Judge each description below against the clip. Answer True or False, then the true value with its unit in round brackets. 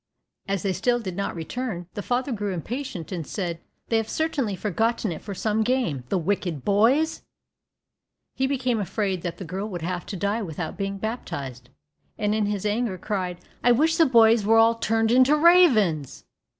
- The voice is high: True (210 Hz)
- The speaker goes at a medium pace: True (180 wpm)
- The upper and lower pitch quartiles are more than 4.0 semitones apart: True (4.7 semitones)